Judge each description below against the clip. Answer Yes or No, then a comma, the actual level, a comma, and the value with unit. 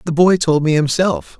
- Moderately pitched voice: Yes, medium, 155 Hz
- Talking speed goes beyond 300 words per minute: No, fast, 215 wpm